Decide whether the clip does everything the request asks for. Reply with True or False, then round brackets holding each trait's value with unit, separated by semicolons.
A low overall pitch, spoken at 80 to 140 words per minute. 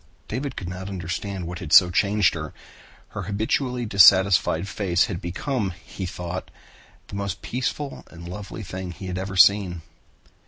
False (95 Hz; 155 wpm)